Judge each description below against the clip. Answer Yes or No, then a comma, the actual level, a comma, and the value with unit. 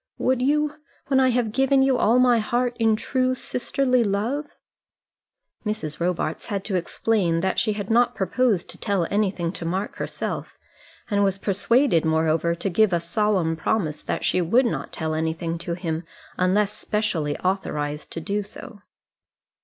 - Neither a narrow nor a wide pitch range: No, wide, 6.0 semitones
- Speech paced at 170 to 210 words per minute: No, average, 160 wpm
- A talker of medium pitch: No, high, 200 Hz